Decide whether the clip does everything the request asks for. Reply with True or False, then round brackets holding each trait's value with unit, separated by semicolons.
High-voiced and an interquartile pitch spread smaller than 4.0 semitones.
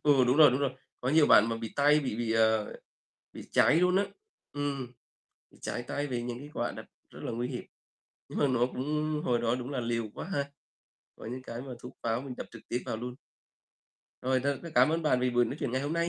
False (125 Hz; 3.3 semitones)